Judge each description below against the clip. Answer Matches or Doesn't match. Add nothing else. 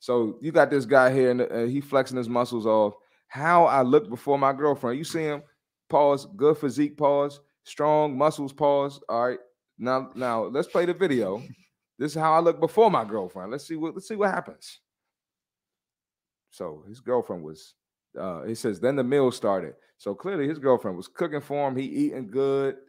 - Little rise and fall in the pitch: Doesn't match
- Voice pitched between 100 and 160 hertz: Matches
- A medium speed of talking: Matches